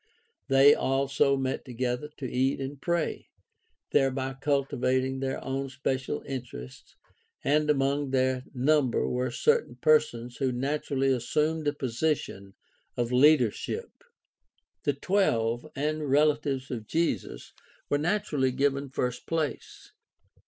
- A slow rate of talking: Yes, slow, 115 wpm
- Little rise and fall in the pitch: Yes, narrow, 2.3 semitones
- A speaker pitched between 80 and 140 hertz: Yes, low, 135 Hz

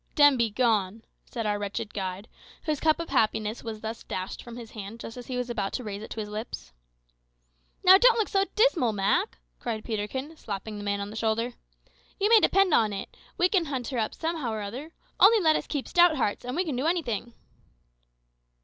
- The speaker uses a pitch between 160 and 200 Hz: No, high, 235 Hz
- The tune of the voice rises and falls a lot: Yes, wide, 6.8 semitones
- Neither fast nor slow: No, fast, 210 wpm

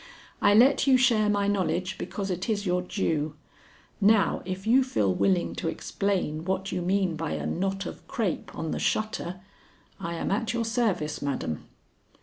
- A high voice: Yes, high, 195 Hz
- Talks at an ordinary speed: Yes, average, 170 wpm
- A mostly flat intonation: No, average, 3.9 semitones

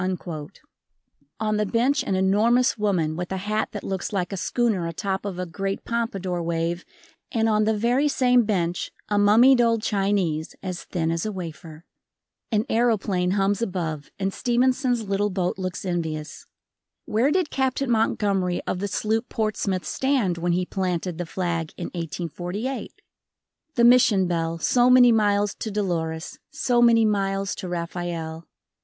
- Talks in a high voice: Yes, high, 195 Hz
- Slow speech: No, average, 155 wpm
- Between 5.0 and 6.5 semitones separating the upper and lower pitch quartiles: No, average, 4.3 semitones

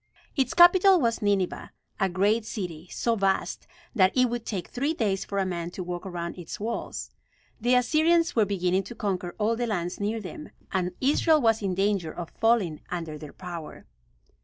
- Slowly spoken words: No, average, 185 wpm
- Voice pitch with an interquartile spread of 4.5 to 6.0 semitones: Yes, average, 4.8 semitones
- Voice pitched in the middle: No, high, 200 Hz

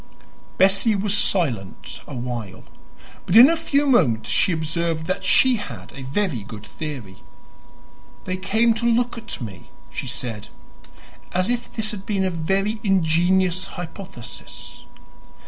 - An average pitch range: No, wide, 7.3 semitones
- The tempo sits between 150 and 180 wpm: No, average, 140 wpm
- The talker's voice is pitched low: No, medium, 185 Hz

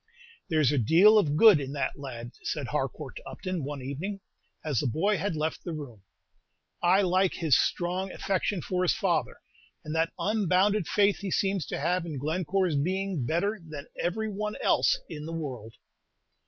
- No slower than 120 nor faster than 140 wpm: No, average, 175 wpm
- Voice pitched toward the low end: No, medium, 175 Hz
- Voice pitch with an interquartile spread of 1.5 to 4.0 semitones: No, average, 4.8 semitones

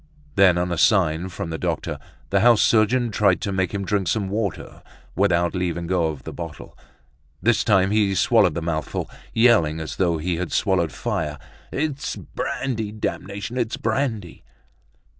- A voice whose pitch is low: Yes, very low, 95 Hz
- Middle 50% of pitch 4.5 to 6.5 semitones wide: No, average, 4.1 semitones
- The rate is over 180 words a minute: No, average, 160 wpm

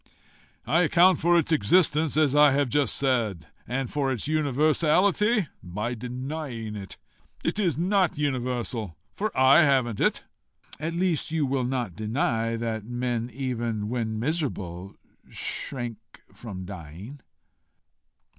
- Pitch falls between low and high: No, low, 130 Hz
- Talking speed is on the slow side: Yes, slow, 125 wpm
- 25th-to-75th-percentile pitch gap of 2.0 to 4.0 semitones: No, average, 5.3 semitones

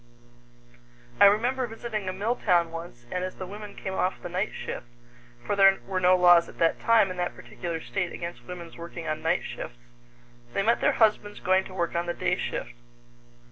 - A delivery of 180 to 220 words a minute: Yes, average, 200 wpm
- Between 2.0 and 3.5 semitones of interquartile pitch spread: Yes, average, 3.0 semitones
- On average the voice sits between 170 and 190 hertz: Yes, medium, 185 Hz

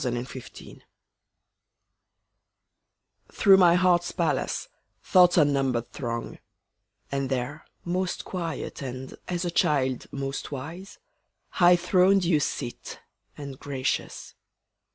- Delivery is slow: Yes, slow, 105 wpm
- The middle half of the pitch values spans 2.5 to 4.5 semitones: No, average, 5.1 semitones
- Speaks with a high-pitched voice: No, medium, 150 Hz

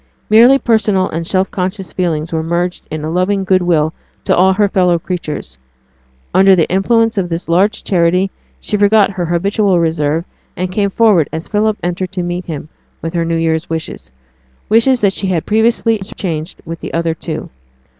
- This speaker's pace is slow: No, average, 180 wpm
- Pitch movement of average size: Yes, average, 3.4 semitones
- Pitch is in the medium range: Yes, medium, 180 Hz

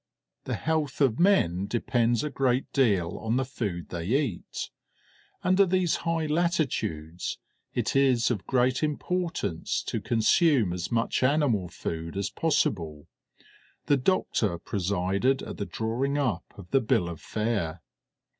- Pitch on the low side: Yes, low, 120 Hz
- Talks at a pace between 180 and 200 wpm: No, slow, 135 wpm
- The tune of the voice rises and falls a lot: Yes, wide, 7.5 semitones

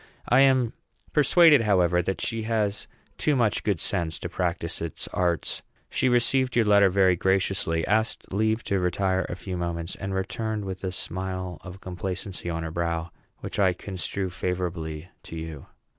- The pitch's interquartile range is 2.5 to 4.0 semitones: Yes, average, 3.5 semitones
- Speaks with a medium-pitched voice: No, very low, 95 Hz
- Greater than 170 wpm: No, average, 165 wpm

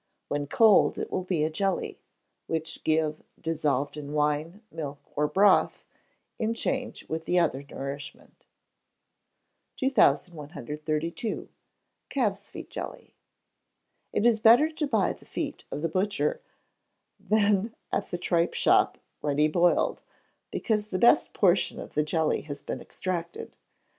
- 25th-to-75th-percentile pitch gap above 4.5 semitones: Yes, wide, 5.4 semitones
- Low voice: No, medium, 170 Hz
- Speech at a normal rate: No, slow, 130 wpm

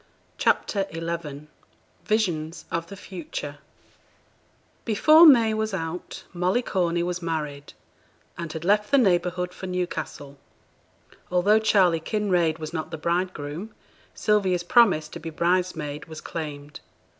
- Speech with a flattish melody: No, average, 3.6 semitones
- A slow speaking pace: Yes, slow, 120 wpm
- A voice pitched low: No, medium, 175 Hz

